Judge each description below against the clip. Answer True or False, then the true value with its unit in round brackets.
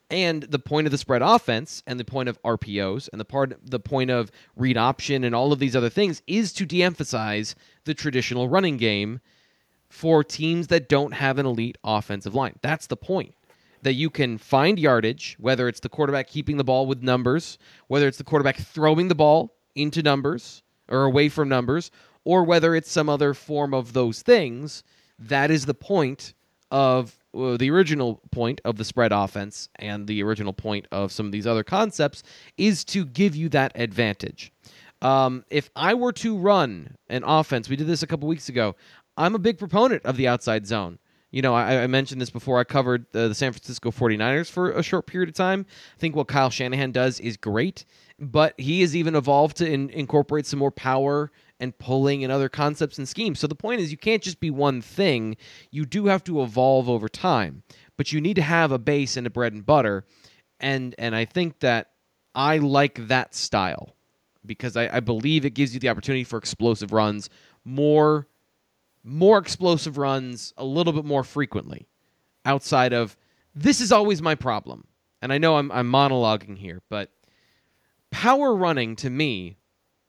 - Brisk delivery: False (195 wpm)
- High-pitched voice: False (135 Hz)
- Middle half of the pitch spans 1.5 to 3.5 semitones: False (4.4 semitones)